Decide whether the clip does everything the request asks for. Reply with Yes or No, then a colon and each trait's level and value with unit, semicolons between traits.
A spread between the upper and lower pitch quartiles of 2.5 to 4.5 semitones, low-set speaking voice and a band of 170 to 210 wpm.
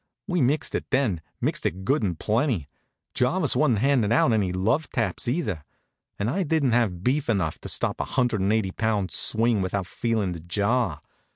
No: average, 5.2 semitones; low, 110 Hz; average, 185 wpm